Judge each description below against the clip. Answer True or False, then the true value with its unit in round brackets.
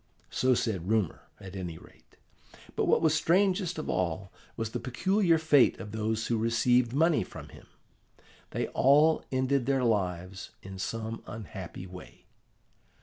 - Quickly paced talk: False (145 wpm)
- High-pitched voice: False (115 Hz)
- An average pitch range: False (7.0 semitones)